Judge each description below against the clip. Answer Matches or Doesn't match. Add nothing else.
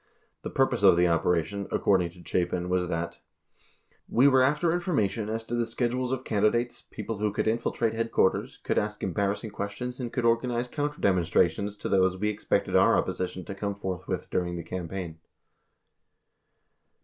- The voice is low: Matches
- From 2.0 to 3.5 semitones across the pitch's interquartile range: Doesn't match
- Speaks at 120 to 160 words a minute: Doesn't match